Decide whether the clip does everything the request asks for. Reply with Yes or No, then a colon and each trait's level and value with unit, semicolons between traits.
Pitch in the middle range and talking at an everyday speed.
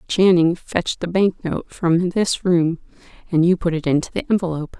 Yes: medium, 175 Hz; average, 190 wpm